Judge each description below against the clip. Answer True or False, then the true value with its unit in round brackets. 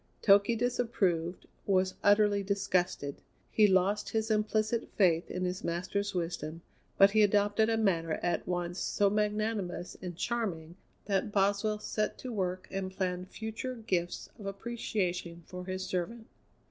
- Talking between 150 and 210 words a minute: False (140 wpm)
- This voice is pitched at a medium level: False (195 Hz)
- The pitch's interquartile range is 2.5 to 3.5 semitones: True (2.9 semitones)